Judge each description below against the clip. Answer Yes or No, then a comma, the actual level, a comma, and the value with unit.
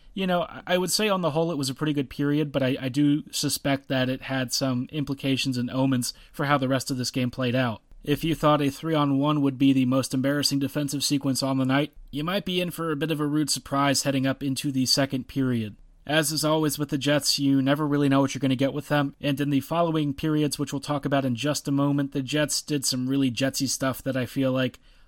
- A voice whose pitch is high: No, medium, 140 Hz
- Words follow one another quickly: Yes, fast, 265 wpm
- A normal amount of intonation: No, narrow, 1.9 semitones